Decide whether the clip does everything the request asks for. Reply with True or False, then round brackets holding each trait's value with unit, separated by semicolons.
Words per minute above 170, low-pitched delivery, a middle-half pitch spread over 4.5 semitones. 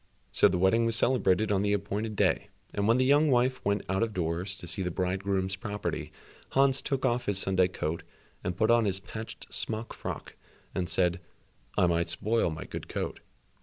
False (195 wpm; 100 Hz; 3.7 semitones)